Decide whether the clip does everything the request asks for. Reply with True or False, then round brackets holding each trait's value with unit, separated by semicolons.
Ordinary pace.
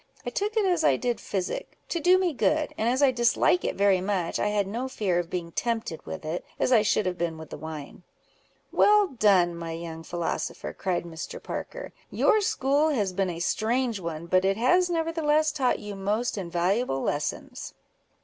True (190 wpm)